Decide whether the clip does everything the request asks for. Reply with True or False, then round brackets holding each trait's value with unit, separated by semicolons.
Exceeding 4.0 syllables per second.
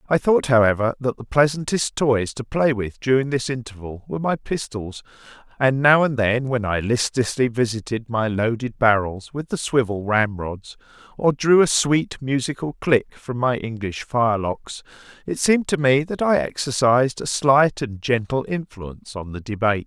True (4.8 syllables/s)